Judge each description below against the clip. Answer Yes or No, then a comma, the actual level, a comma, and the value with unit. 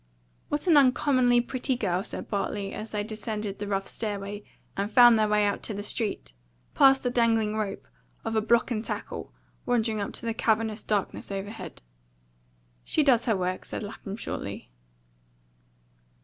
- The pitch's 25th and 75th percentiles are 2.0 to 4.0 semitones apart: Yes, average, 2.7 semitones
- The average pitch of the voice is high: Yes, high, 215 Hz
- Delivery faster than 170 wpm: No, average, 165 wpm